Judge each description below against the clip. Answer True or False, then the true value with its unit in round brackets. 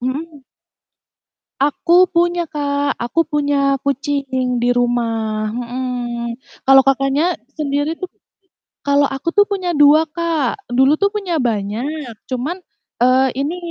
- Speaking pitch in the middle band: False (280 Hz)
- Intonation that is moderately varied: True (4.2 semitones)